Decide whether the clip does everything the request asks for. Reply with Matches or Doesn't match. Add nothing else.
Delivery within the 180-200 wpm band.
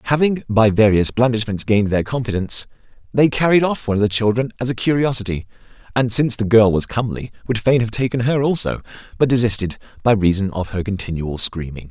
Matches